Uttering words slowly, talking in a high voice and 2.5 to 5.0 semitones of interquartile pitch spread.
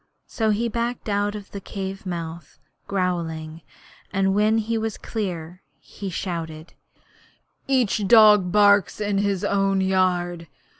Yes: slow, 130 wpm; high, 195 Hz; average, 3.0 semitones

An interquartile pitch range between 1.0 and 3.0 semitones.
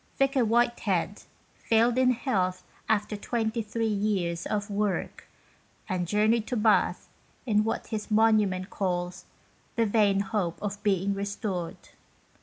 Yes: narrow, 2.5 semitones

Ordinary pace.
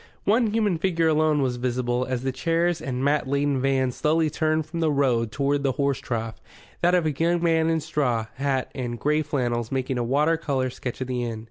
No: fast, 215 wpm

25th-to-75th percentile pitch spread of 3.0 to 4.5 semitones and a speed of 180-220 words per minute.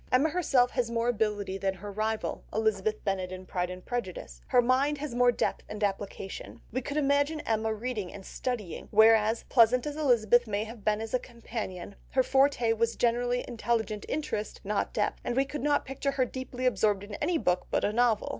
Yes: average, 3.5 semitones; average, 195 wpm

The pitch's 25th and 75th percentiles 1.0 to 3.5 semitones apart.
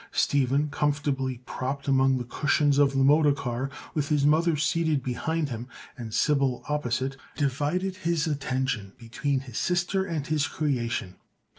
Yes: average, 2.7 semitones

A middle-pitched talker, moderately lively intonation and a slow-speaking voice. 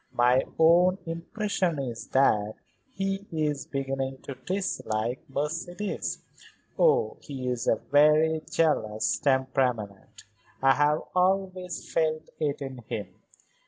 Yes: medium, 145 Hz; average, 4.8 semitones; slow, 110 wpm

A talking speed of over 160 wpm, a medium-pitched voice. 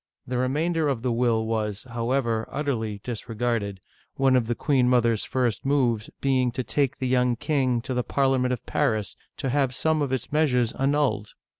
No: average, 180 wpm; low, 125 Hz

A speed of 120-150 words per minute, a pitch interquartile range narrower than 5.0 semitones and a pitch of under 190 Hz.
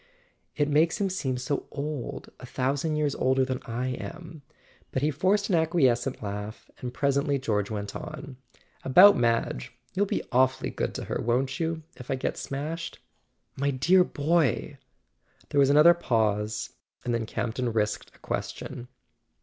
No: average, 160 wpm; average, 4.3 semitones; low, 135 Hz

